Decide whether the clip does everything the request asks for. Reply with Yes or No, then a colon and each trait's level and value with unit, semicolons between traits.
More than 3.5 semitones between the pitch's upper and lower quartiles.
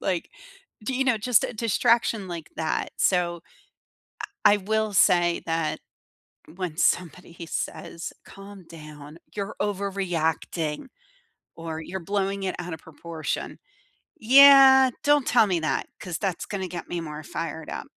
Yes: average, 4.1 semitones